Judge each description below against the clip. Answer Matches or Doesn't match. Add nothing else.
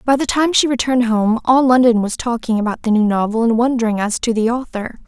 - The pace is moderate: Doesn't match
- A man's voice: Doesn't match